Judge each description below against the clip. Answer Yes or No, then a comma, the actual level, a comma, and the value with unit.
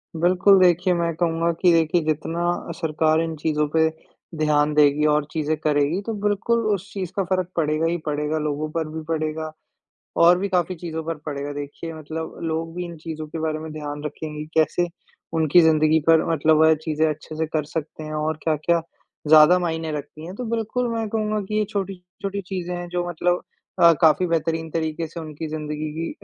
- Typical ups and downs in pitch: No, narrow, 2.3 semitones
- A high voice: No, medium, 160 Hz